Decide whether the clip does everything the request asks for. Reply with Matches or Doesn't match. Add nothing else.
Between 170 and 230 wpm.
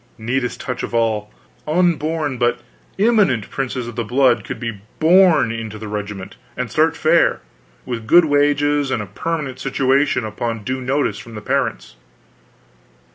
Doesn't match